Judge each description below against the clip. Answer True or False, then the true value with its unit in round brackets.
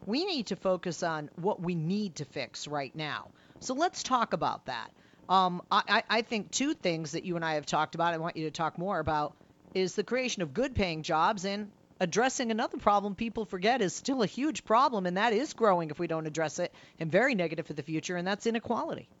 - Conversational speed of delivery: False (230 wpm)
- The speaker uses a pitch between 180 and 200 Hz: True (185 Hz)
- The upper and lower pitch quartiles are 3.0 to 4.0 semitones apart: False (5.3 semitones)